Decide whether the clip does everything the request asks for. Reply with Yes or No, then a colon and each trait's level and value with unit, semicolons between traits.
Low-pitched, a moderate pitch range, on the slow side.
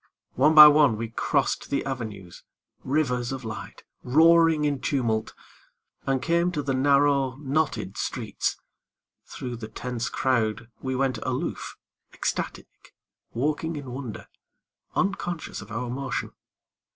Yes: low, 130 Hz; average, 3.8 semitones; slow, 125 wpm